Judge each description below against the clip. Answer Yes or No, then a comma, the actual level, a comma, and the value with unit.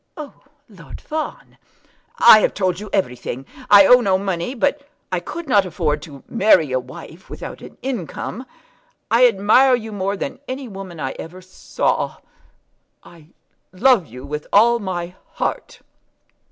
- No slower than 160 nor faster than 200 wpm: No, average, 150 wpm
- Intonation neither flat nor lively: No, wide, 6.0 semitones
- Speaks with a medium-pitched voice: No, high, 195 Hz